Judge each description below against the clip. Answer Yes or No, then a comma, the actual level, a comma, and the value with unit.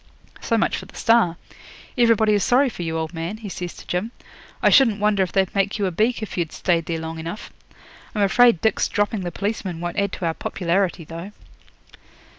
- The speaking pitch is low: No, high, 195 Hz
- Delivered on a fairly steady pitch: No, average, 4.1 semitones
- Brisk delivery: Yes, fast, 210 wpm